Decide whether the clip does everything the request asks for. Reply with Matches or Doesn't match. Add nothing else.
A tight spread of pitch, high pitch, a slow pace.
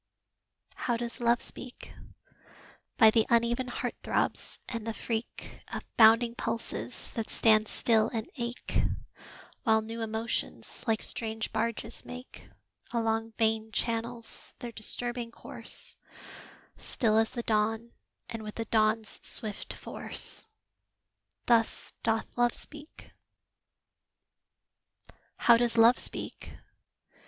Matches